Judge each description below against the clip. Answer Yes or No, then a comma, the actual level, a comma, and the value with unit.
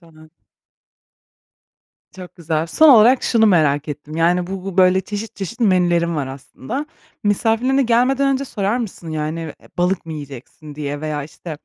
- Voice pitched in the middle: Yes, medium, 180 Hz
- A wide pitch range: Yes, wide, 6.2 semitones